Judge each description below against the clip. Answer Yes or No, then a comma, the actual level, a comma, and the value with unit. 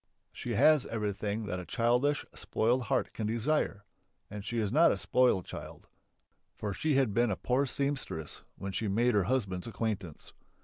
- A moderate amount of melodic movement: Yes, average, 4.0 semitones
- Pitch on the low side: Yes, low, 115 Hz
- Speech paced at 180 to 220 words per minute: No, average, 170 wpm